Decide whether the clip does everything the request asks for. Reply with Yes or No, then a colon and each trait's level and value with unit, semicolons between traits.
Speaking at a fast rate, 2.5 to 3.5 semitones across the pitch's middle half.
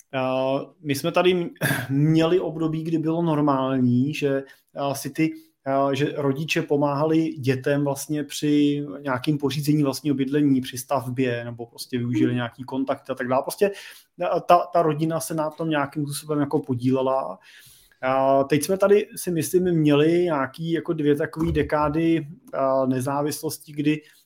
No: average, 135 wpm; average, 2.8 semitones